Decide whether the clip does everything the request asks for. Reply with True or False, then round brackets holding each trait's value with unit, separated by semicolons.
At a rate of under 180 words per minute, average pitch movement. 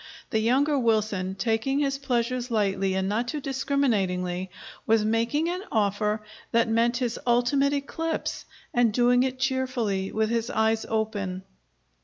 True (140 wpm; 3.6 semitones)